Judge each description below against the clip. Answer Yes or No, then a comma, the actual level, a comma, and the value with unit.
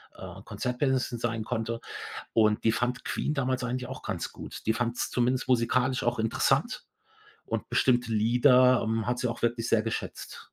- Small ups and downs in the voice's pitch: Yes, narrow, 1.8 semitones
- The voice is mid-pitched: No, low, 120 Hz